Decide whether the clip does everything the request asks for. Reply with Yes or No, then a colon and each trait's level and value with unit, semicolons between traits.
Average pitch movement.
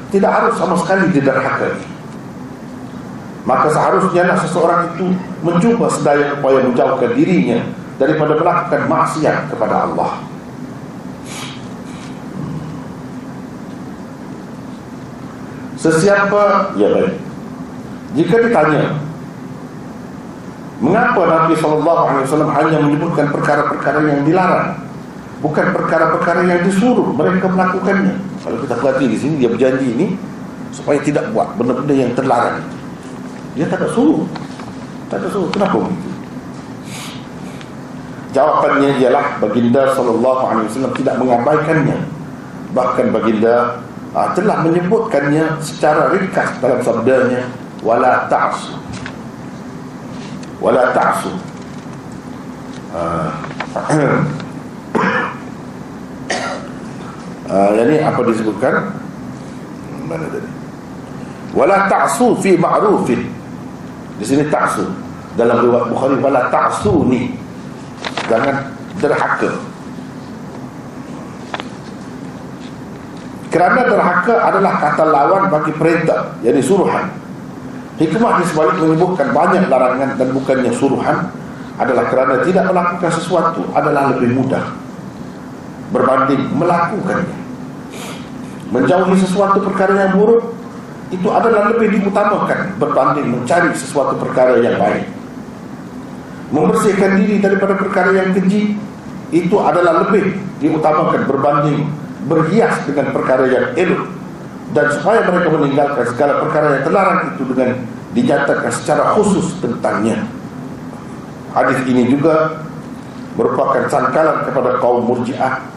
No: wide, 6.2 semitones